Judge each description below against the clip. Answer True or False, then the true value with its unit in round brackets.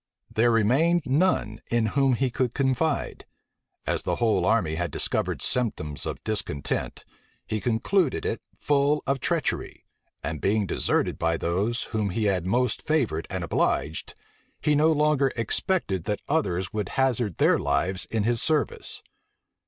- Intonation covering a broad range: True (6.1 semitones)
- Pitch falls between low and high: False (115 Hz)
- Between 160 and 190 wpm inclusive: False (145 wpm)